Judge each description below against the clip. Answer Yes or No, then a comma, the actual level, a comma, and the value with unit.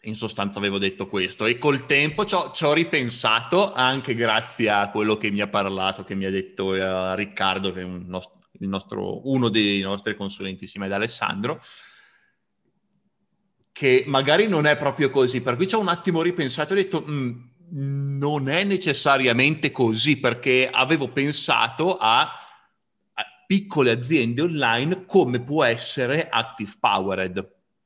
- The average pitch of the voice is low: Yes, low, 130 Hz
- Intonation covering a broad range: Yes, wide, 7.2 semitones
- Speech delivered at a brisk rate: No, average, 155 wpm